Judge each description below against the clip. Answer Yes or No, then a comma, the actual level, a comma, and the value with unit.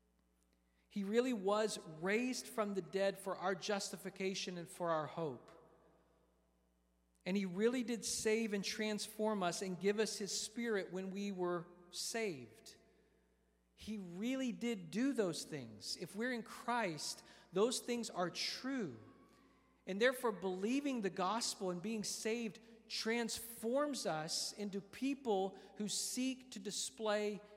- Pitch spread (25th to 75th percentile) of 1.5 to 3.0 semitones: No, average, 4.1 semitones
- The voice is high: Yes, high, 200 Hz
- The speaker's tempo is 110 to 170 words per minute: Yes, slow, 135 wpm